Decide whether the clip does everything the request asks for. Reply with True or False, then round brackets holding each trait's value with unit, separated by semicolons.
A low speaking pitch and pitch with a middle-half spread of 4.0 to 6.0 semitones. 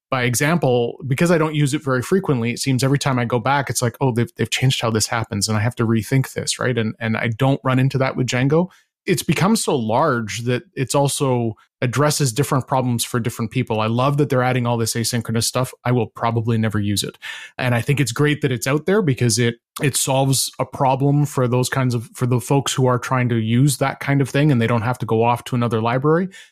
False (125 Hz; 2.9 semitones)